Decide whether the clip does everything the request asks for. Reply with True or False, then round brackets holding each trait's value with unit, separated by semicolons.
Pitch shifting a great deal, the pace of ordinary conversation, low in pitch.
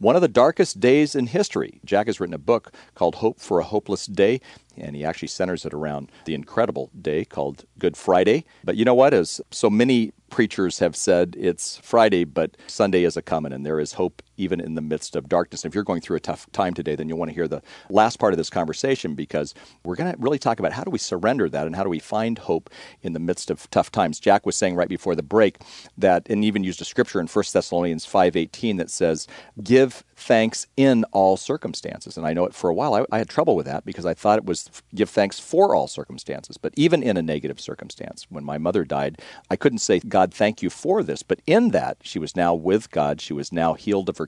False (6.1 semitones; 245 wpm; 95 Hz)